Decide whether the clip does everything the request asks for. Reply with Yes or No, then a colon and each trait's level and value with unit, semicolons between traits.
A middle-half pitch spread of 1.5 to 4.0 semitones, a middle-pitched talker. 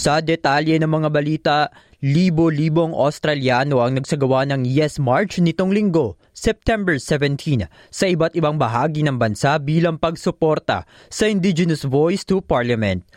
Yes: average, 3.4 semitones; medium, 155 Hz